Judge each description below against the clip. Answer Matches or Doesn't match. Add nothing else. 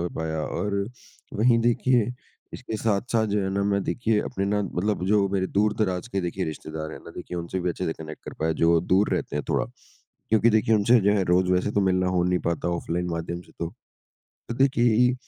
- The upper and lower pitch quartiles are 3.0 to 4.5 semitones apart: Matches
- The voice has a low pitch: Matches